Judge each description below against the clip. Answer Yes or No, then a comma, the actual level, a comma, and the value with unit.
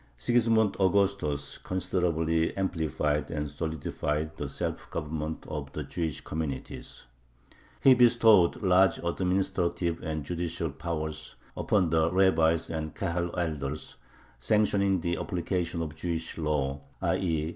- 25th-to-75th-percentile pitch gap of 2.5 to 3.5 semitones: Yes, average, 3.1 semitones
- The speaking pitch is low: Yes, very low, 85 Hz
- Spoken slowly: Yes, slow, 115 wpm